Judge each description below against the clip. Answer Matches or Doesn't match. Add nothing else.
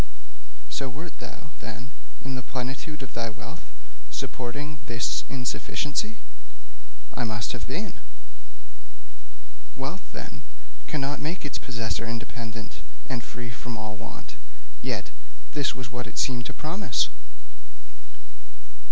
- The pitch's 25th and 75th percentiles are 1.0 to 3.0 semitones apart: Doesn't match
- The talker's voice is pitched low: Matches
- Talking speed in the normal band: Doesn't match